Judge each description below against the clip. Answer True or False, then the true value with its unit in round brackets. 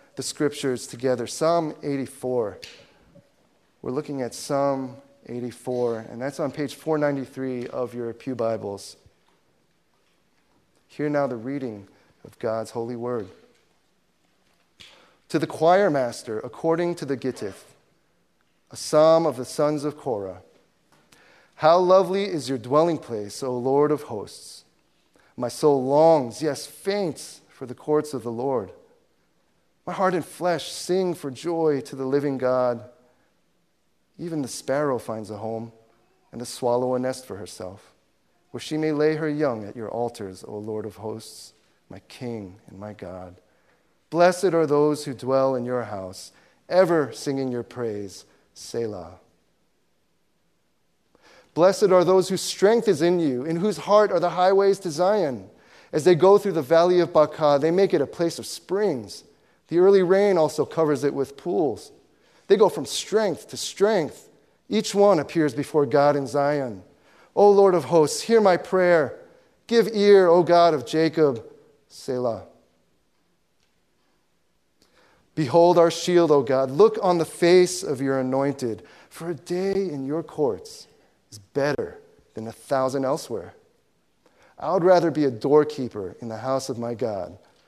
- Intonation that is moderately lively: False (5.9 semitones)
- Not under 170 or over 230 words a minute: False (150 wpm)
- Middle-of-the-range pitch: True (145 Hz)